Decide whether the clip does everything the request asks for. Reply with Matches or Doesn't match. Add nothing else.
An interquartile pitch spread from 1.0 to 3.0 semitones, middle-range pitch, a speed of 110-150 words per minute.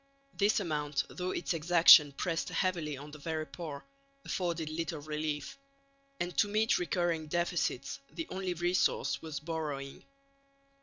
Matches